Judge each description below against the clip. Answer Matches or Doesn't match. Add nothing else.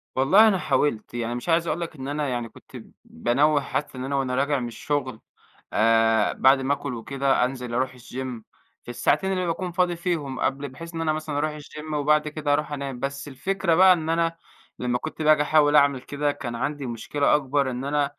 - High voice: Doesn't match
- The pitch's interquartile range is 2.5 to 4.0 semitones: Matches